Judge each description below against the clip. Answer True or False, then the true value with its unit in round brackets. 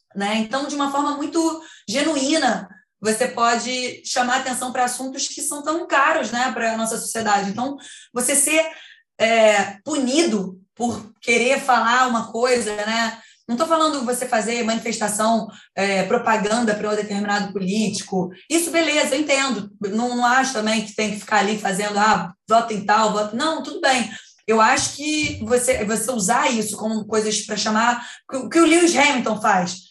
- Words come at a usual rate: True (165 wpm)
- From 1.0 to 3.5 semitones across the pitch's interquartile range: False (4.2 semitones)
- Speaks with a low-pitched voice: False (235 Hz)